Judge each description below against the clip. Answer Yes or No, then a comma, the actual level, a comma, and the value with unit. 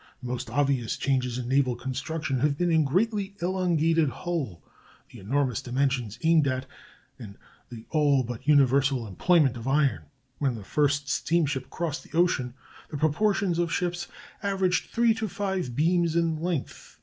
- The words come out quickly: No, average, 160 wpm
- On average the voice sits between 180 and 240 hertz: No, medium, 145 Hz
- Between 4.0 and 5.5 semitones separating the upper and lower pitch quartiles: Yes, average, 5.1 semitones